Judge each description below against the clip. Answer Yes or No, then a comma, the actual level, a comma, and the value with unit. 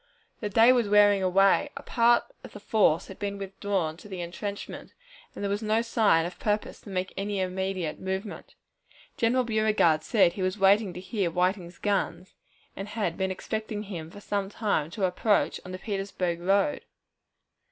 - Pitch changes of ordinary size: No, narrow, 2.3 semitones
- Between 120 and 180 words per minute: Yes, average, 175 wpm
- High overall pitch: Yes, high, 195 Hz